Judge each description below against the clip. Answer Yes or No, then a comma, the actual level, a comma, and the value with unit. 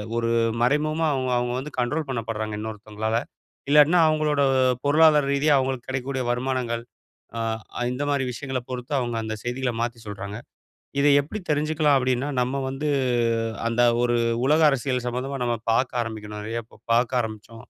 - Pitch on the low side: Yes, low, 125 Hz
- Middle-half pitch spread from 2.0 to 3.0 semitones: No, average, 3.5 semitones